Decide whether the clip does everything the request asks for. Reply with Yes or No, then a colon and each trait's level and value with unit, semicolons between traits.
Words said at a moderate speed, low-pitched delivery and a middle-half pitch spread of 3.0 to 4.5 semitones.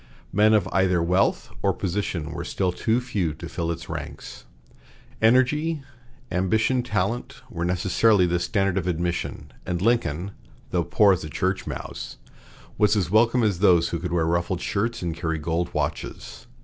Yes: average, 160 wpm; very low, 90 Hz; average, 4.1 semitones